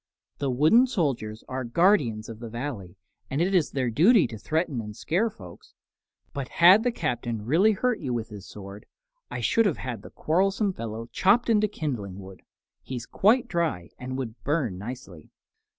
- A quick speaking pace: No, average, 175 wpm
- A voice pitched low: Yes, low, 130 Hz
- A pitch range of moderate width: No, wide, 8.7 semitones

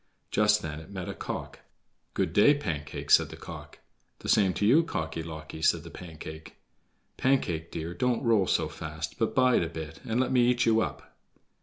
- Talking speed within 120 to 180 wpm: No, average, 190 wpm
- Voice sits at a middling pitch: No, very low, 90 Hz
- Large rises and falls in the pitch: Yes, wide, 6.6 semitones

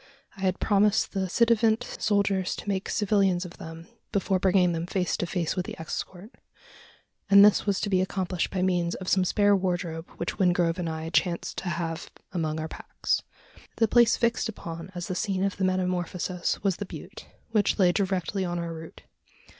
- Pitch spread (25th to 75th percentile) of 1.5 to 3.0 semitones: Yes, narrow, 2.4 semitones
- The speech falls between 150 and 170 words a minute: No, average, 190 wpm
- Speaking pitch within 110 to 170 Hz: No, medium, 185 Hz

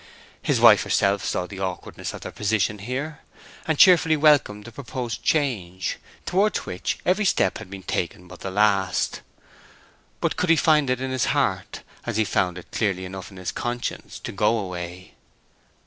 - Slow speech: No, average, 165 wpm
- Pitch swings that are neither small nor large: No, wide, 6.4 semitones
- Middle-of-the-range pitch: No, low, 105 Hz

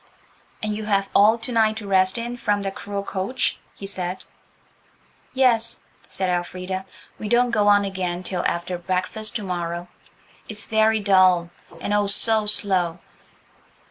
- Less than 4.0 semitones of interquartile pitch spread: Yes, average, 2.9 semitones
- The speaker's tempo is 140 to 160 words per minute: Yes, average, 145 wpm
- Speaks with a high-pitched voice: Yes, high, 200 Hz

